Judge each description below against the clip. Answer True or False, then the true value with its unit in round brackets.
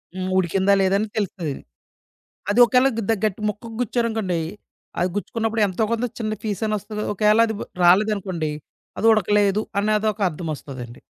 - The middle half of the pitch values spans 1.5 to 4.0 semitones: True (2.9 semitones)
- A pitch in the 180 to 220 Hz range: True (210 Hz)